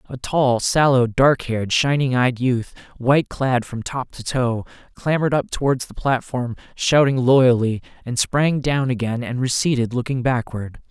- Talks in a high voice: No, low, 125 Hz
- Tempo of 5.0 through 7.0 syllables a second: No, 4.5 syllables/s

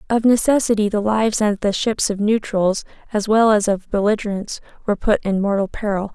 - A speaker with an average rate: Yes, average, 185 wpm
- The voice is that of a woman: Yes, female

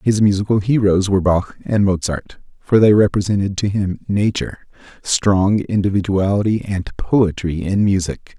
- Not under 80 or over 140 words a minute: Yes, slow, 135 wpm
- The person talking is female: No, male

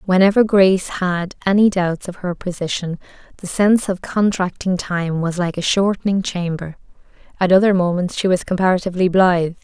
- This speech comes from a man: No, female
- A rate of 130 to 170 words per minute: Yes, average, 155 wpm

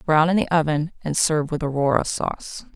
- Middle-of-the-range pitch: Yes, medium, 155 Hz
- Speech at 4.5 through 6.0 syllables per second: Yes, 5.7 syllables/s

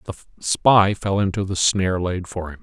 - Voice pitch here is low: Yes, very low, 95 Hz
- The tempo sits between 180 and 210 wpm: Yes, fast, 205 wpm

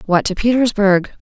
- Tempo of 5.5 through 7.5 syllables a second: No, 5.1 syllables/s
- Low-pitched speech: No, high, 205 Hz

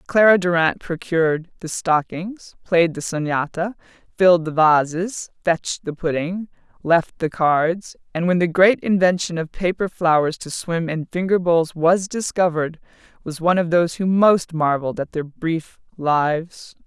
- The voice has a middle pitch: Yes, medium, 170 Hz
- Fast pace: No, average, 155 wpm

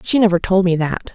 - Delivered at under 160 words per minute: No, fast, 260 wpm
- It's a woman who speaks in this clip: Yes, female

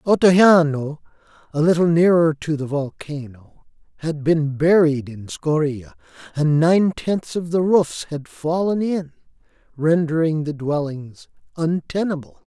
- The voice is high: No, medium, 160 Hz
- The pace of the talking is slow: Yes, slow, 120 wpm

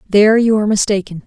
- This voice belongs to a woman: Yes, female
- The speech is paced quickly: No, average, 190 wpm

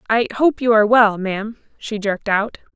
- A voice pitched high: Yes, high, 220 Hz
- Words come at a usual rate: Yes, average, 195 wpm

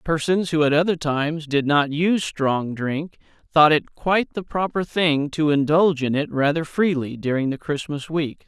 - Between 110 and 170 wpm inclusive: No, average, 185 wpm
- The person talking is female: No, male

